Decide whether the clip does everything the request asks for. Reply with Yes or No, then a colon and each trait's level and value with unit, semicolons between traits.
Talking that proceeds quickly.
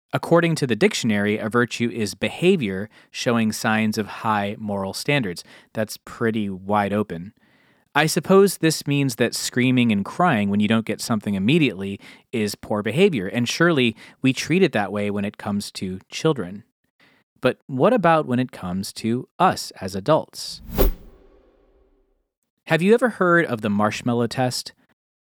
No: average, 155 wpm